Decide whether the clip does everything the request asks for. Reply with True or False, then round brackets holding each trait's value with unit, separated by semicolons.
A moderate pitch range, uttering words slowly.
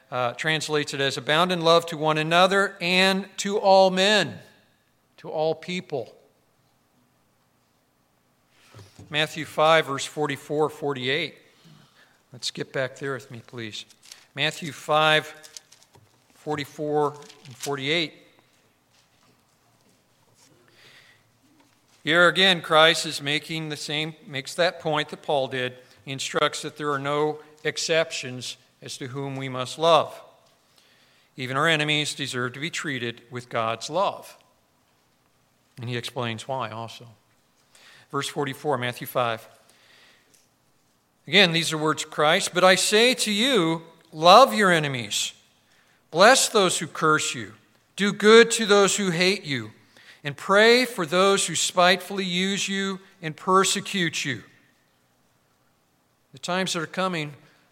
True (4.8 semitones; 125 wpm)